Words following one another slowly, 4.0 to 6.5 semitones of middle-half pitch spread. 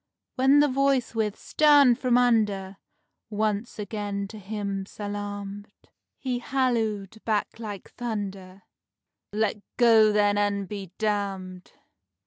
No: slow, 110 wpm; average, 2.8 semitones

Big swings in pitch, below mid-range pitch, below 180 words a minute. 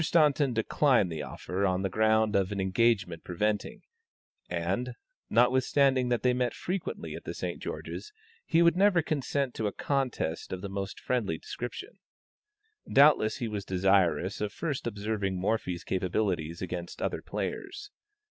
Yes: wide, 5.7 semitones; low, 110 Hz; average, 150 wpm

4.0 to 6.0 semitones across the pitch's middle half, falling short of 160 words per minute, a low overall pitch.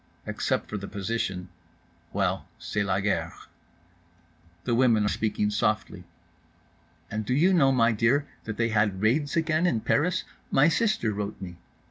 Yes: average, 5.0 semitones; average, 145 wpm; low, 110 Hz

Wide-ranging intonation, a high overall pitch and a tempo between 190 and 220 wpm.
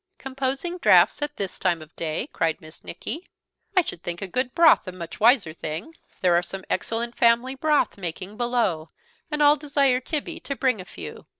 Yes: wide, 8.1 semitones; high, 235 Hz; average, 195 wpm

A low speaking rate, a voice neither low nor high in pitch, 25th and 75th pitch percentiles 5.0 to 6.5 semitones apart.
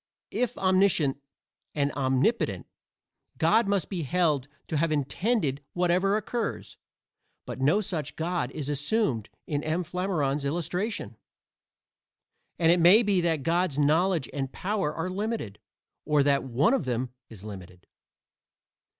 Yes: slow, 130 wpm; medium, 160 Hz; average, 5.3 semitones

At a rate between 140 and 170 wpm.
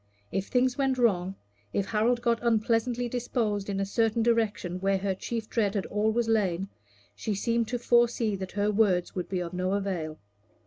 No: average, 180 wpm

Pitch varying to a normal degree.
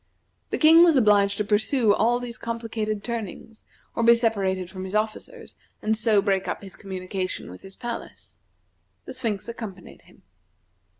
Yes: average, 3.0 semitones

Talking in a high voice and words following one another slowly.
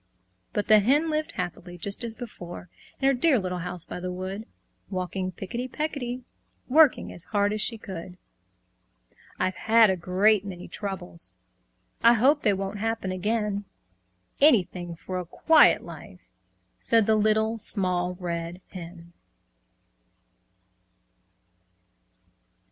Yes: high, 200 Hz; slow, 125 wpm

